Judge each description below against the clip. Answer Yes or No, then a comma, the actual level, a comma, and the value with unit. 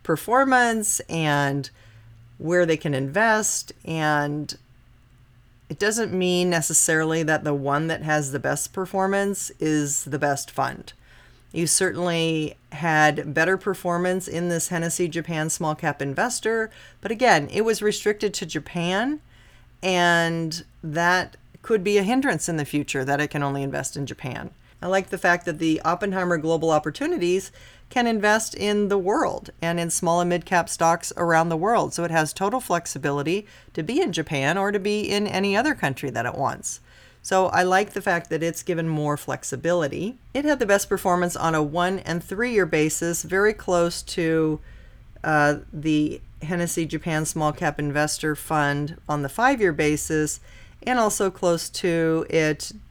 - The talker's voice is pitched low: No, medium, 165 Hz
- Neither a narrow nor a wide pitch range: Yes, average, 4.1 semitones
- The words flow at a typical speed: Yes, average, 165 wpm